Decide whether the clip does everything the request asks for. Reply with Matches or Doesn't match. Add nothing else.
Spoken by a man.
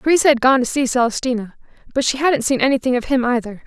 Doesn't match